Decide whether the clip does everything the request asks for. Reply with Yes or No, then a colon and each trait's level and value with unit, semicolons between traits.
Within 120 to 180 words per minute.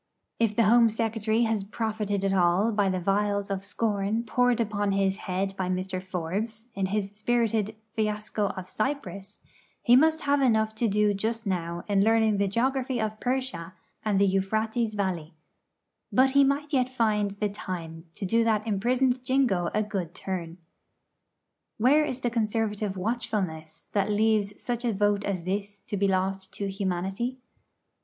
Yes: average, 165 wpm